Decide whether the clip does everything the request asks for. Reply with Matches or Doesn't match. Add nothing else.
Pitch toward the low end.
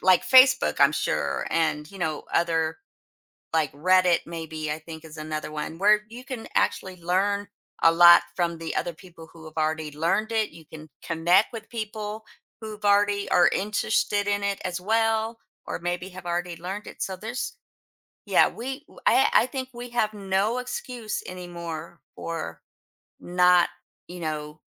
Doesn't match